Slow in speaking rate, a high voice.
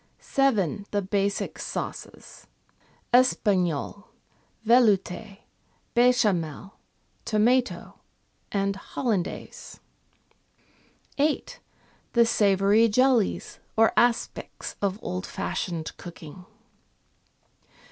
Yes: slow, 65 wpm; high, 205 Hz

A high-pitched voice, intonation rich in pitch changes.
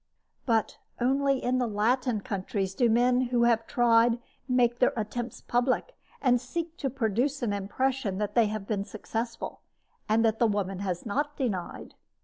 No: high, 235 Hz; average, 3.2 semitones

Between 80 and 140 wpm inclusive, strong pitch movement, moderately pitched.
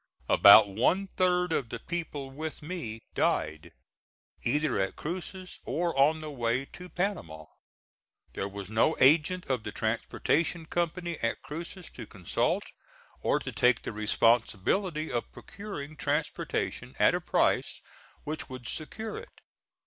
Yes: slow, 135 wpm; wide, 7.2 semitones; medium, 150 Hz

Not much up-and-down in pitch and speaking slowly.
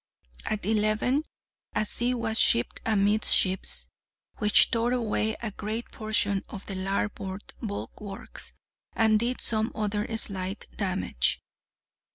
Yes: narrow, 2.0 semitones; slow, 115 wpm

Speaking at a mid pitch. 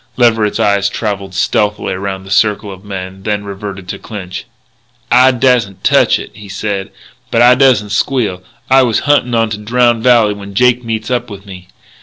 No: low, 105 Hz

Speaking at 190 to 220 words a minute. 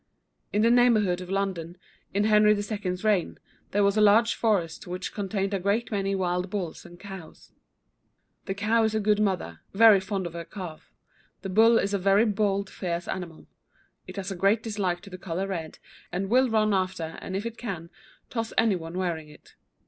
Yes: average, 200 wpm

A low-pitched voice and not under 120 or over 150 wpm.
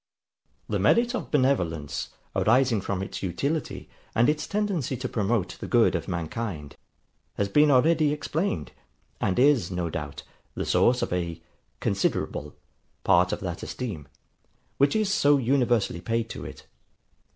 Yes: low, 115 Hz; average, 140 wpm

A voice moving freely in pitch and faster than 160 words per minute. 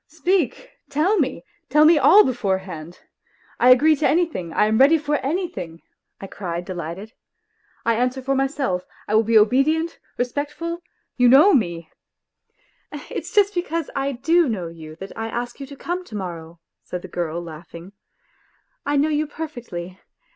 Yes: wide, 9.0 semitones; average, 170 wpm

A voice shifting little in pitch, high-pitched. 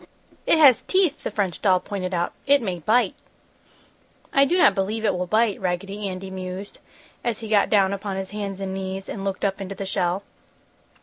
Yes: narrow, 2.3 semitones; high, 195 Hz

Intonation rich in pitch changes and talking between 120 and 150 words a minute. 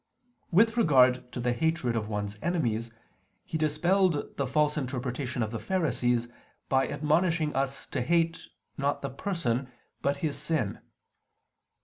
No: average, 4.9 semitones; slow, 135 wpm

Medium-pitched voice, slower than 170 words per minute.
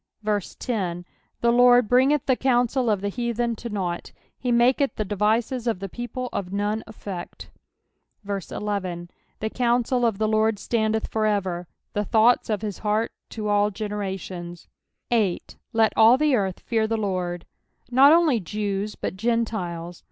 No: high, 215 Hz; average, 155 wpm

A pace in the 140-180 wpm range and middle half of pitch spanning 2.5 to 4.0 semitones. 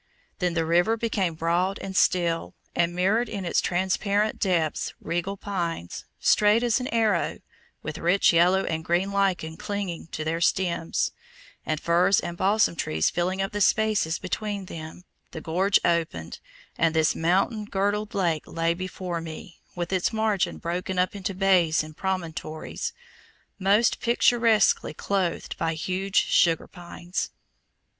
Yes: average, 145 wpm; average, 3.0 semitones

